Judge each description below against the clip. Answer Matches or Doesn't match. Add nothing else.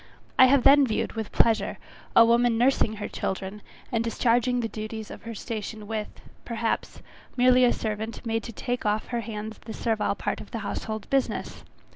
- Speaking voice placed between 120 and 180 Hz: Doesn't match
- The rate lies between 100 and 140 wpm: Doesn't match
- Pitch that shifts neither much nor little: Doesn't match